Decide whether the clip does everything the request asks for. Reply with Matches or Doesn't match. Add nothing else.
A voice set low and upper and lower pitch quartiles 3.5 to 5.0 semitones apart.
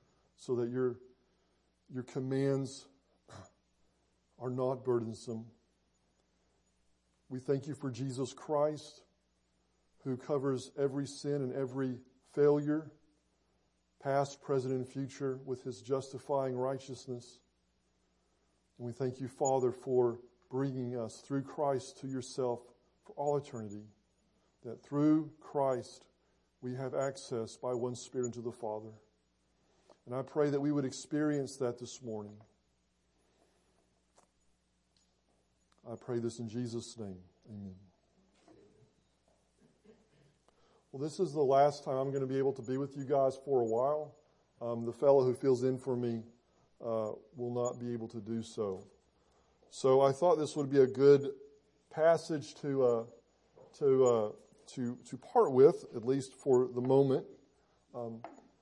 Matches